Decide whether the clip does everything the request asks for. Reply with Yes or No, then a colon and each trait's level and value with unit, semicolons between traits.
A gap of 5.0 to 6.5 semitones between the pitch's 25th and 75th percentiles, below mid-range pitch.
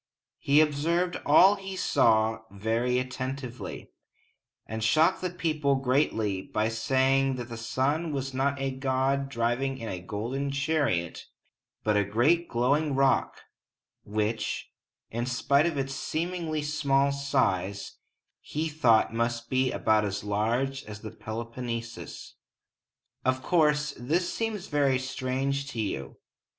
No: average, 4.0 semitones; low, 130 Hz